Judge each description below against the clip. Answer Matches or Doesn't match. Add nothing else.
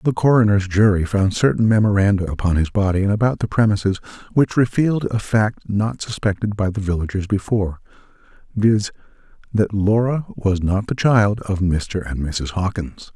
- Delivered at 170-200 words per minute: Doesn't match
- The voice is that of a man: Matches